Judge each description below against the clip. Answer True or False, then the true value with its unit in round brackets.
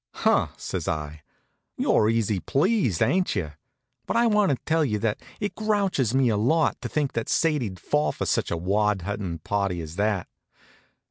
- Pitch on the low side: True (110 Hz)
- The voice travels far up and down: True (9.0 semitones)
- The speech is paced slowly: False (180 wpm)